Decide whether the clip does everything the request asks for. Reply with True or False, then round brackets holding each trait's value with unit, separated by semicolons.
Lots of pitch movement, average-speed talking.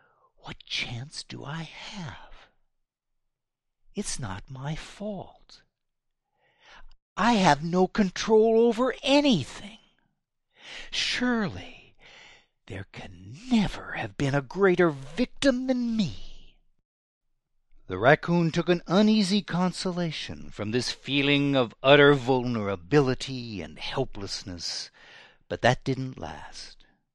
False (8.2 semitones; 95 wpm)